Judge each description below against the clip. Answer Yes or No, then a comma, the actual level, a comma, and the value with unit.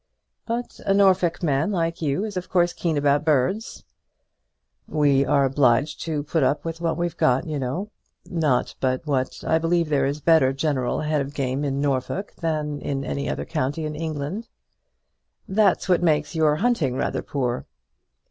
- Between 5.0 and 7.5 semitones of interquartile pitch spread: No, average, 3.5 semitones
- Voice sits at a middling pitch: Yes, medium, 150 Hz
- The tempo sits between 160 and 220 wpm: Yes, average, 175 wpm